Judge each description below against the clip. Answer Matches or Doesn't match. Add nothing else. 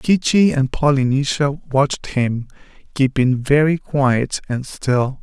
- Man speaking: Matches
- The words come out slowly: Matches